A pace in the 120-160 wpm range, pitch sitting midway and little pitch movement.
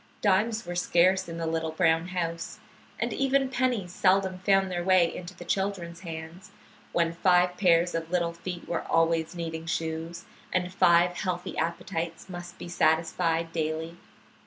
Yes: average, 155 wpm; medium, 175 Hz; narrow, 2.0 semitones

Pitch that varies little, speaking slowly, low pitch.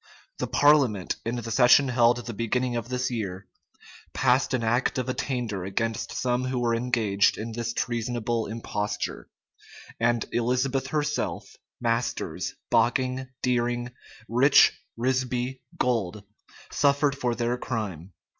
Yes: narrow, 1.9 semitones; slow, 125 wpm; low, 120 Hz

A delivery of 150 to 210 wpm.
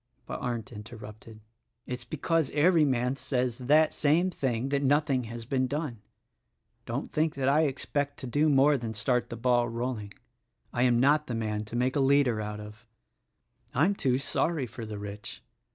Yes: average, 175 wpm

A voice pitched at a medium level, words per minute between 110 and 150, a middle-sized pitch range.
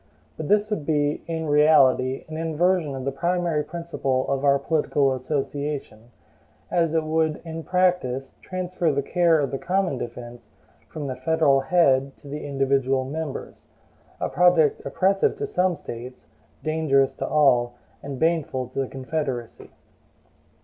Yes: medium, 150 Hz; average, 145 wpm; average, 3.5 semitones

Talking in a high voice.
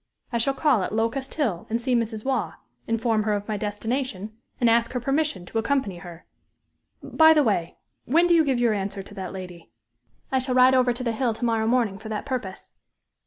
Yes: high, 230 Hz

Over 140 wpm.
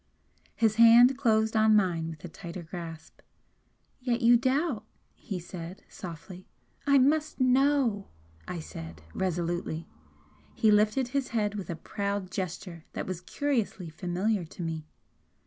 No: slow, 135 wpm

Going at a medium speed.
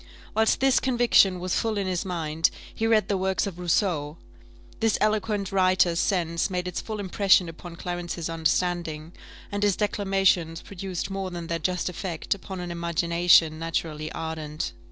Yes: average, 155 wpm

